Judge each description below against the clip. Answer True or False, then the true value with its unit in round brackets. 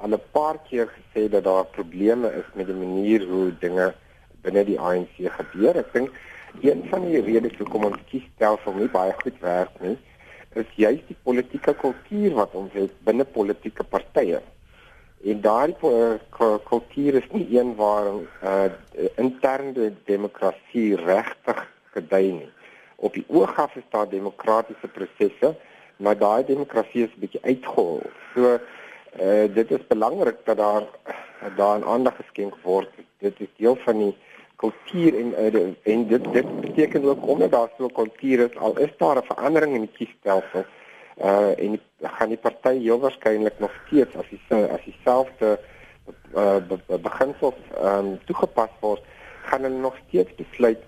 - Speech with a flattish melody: False (3.7 semitones)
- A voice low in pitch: True (110 Hz)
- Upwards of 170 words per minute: False (160 wpm)